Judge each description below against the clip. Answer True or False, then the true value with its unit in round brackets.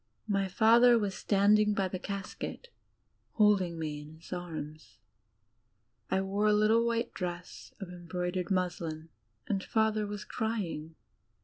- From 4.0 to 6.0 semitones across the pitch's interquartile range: False (3.3 semitones)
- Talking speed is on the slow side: True (130 wpm)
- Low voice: False (195 Hz)